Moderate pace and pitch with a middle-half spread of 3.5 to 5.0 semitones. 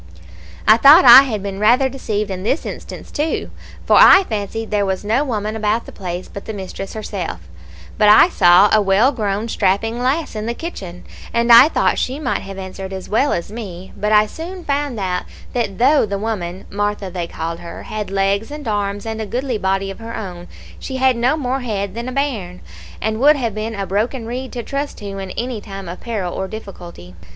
No: fast, 210 wpm; average, 4.2 semitones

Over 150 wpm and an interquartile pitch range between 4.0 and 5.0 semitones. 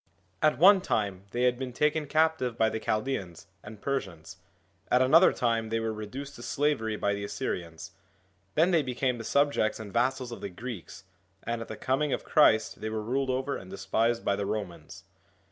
Yes: average, 190 wpm; average, 4.3 semitones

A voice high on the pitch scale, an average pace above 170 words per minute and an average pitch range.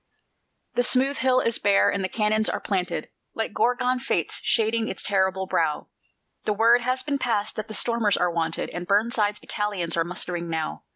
Yes: high, 210 Hz; average, 180 wpm; average, 3.9 semitones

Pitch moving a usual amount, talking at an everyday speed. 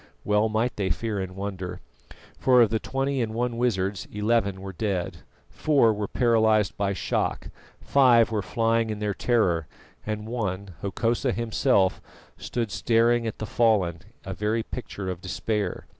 Yes: average, 3.1 semitones; average, 155 wpm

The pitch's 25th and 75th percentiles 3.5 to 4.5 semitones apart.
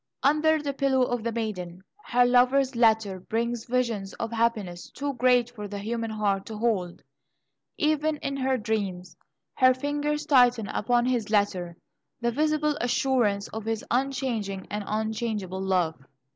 Yes: average, 3.9 semitones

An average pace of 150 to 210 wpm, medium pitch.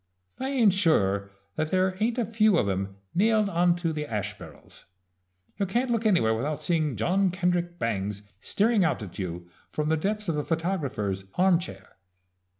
Yes: average, 170 wpm; medium, 170 Hz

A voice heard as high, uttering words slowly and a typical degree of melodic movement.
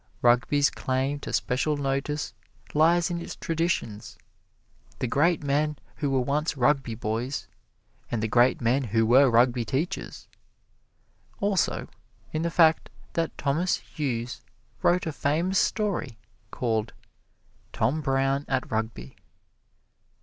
No: medium, 140 Hz; slow, 120 wpm; average, 4.5 semitones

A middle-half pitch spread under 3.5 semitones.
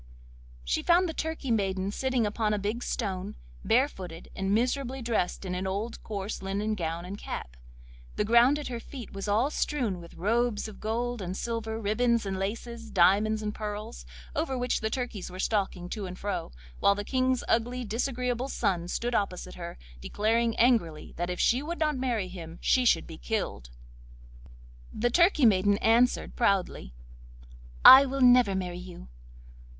No: average, 4.2 semitones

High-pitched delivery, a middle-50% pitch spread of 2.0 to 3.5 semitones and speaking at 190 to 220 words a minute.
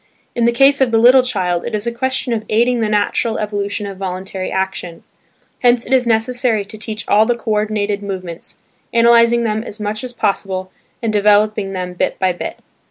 Yes: high, 215 Hz; average, 3.0 semitones; average, 195 wpm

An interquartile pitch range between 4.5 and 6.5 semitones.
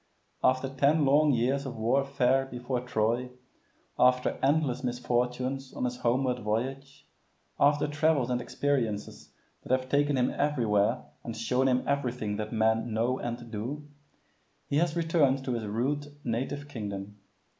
No: average, 2.9 semitones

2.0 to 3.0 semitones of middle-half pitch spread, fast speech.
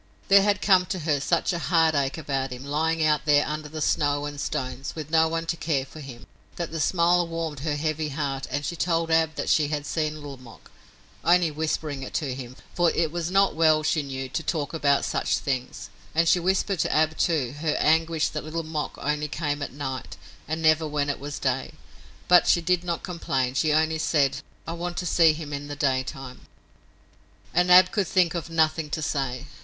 Yes: narrow, 2.6 semitones; fast, 210 wpm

